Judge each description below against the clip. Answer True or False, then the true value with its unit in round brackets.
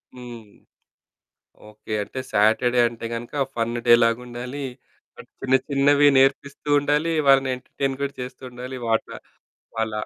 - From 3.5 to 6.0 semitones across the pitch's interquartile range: False (2.9 semitones)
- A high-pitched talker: False (125 Hz)